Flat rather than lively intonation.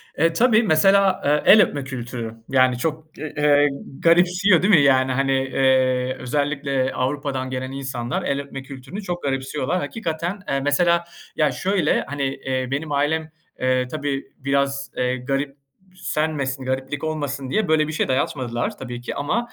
No: average, 3.2 semitones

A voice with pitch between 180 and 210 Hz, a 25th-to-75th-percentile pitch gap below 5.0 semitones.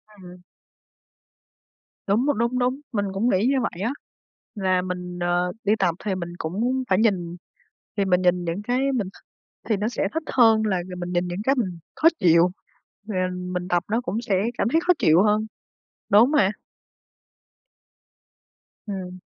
Yes: high, 195 Hz; average, 4.1 semitones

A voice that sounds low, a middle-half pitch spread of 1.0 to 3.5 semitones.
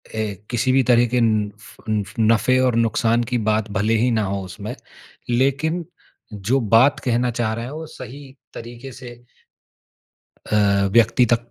Yes: low, 115 Hz; average, 2.9 semitones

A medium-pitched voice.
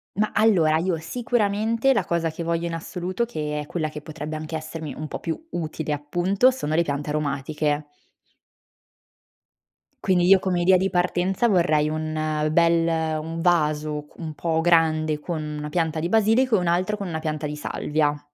Yes: medium, 165 Hz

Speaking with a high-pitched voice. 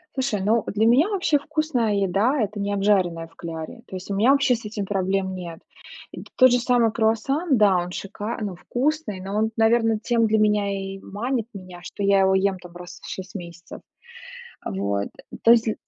Yes: high, 210 Hz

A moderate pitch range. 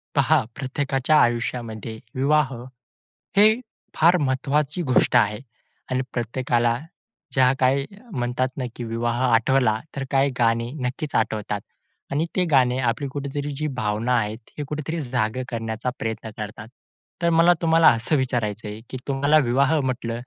Yes: average, 3.7 semitones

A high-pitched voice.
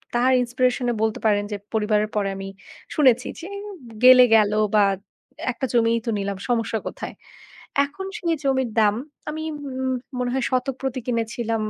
Yes: high, 240 Hz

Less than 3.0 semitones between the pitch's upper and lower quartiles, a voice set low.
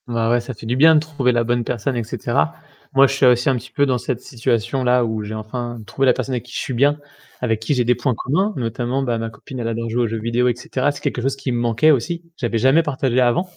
Yes: narrow, 2.5 semitones; low, 125 Hz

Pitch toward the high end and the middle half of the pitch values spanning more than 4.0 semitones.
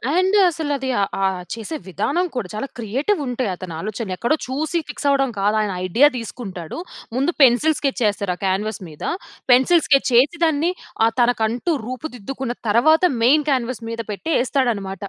Yes: high, 245 Hz; average, 5.2 semitones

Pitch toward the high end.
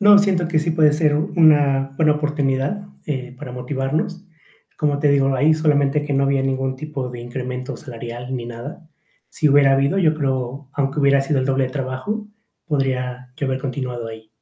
No: medium, 140 Hz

